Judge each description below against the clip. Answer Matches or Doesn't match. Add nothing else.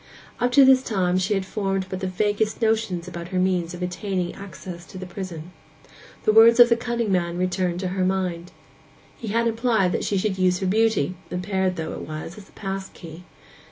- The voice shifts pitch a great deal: Doesn't match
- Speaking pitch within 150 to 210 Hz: Matches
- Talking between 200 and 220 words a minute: Matches